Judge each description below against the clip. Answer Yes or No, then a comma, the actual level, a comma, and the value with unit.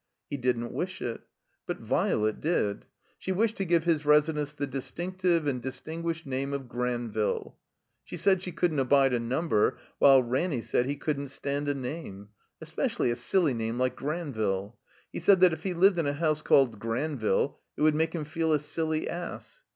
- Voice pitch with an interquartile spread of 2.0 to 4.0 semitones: No, average, 4.9 semitones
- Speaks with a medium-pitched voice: Yes, medium, 145 Hz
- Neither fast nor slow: Yes, average, 180 wpm